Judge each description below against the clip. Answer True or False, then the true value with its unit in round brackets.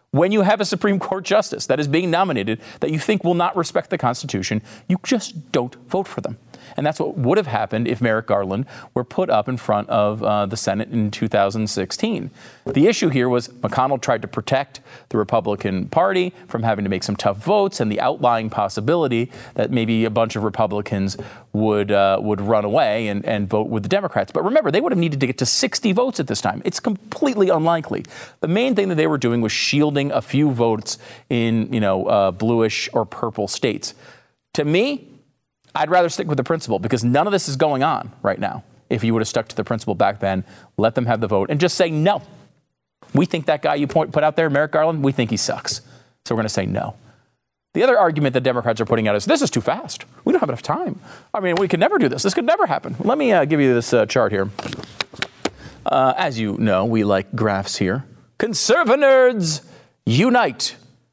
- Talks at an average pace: False (220 wpm)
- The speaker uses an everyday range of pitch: False (7.0 semitones)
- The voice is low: True (125 Hz)